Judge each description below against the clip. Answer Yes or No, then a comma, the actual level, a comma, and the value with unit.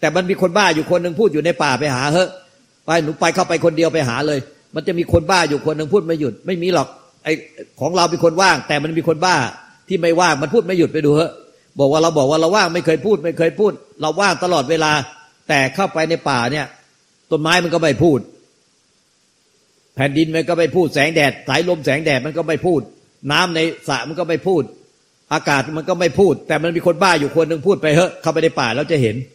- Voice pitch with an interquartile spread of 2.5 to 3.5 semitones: Yes, average, 2.8 semitones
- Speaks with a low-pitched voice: No, medium, 160 Hz